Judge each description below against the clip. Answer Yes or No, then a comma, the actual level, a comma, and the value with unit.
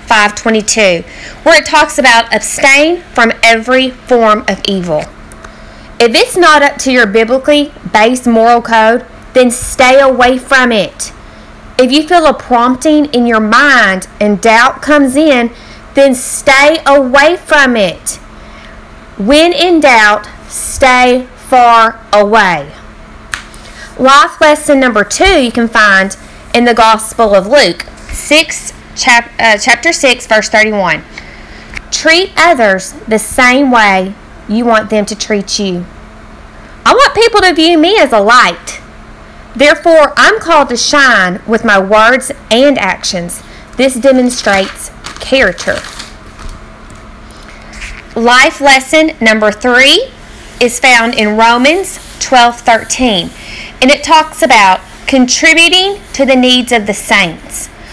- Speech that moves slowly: Yes, slow, 125 wpm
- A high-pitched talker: Yes, very high, 250 Hz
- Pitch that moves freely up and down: No, average, 4.6 semitones